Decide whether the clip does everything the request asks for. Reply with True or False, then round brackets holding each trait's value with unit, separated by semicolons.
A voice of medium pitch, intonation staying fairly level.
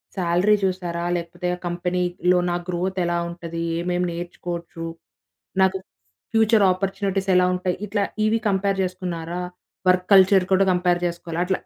True (180 Hz; 1.6 semitones)